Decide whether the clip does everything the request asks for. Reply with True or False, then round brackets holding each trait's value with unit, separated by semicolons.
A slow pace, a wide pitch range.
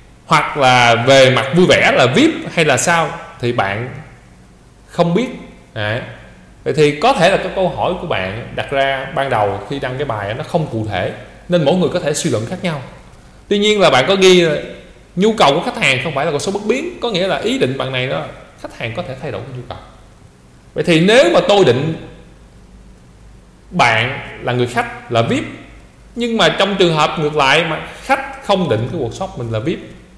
False (220 wpm; 7.5 semitones)